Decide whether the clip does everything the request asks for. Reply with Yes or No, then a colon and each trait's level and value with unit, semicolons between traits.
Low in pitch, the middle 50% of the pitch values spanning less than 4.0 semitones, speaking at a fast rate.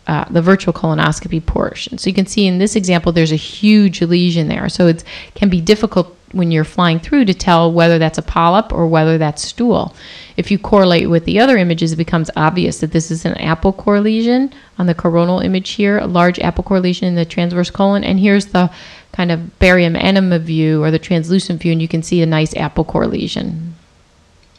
No: medium, 175 Hz; average, 2.9 semitones; fast, 215 wpm